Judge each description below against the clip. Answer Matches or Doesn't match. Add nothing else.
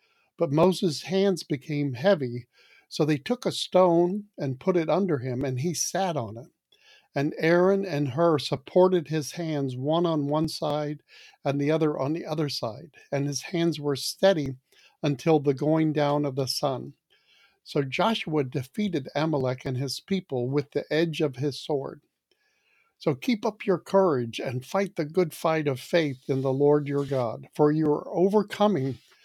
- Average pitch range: Matches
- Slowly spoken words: Doesn't match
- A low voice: Doesn't match